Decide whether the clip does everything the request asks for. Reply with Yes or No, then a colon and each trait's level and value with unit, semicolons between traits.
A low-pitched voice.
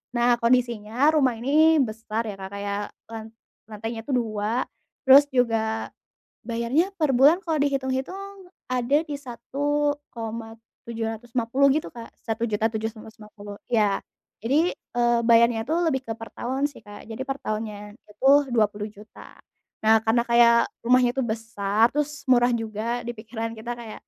No: high, 235 Hz